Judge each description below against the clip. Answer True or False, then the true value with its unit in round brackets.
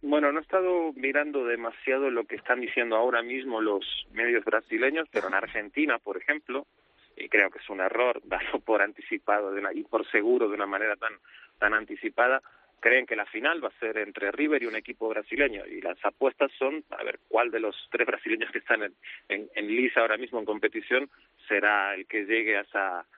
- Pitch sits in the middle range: True (150 Hz)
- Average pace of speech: False (200 wpm)